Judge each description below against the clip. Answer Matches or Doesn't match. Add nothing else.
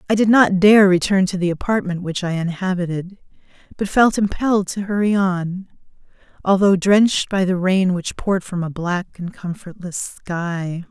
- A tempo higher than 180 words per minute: Doesn't match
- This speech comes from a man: Doesn't match